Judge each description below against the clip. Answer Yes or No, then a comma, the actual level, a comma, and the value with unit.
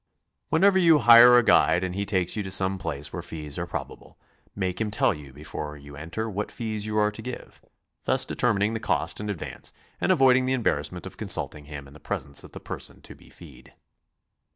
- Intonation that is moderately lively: No, wide, 6.7 semitones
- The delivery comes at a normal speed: No, fast, 210 wpm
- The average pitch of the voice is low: Yes, low, 100 Hz